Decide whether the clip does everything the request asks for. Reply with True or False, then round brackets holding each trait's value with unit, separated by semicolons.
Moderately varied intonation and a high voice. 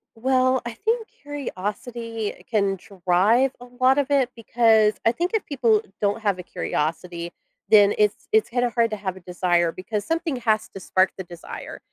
True (5.0 semitones; 220 Hz)